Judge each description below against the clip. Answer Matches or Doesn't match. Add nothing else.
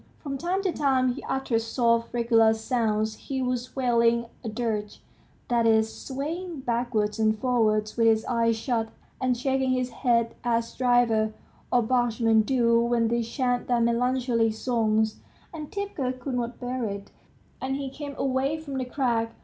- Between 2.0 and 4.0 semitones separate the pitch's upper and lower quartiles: Matches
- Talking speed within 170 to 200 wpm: Doesn't match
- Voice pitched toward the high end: Matches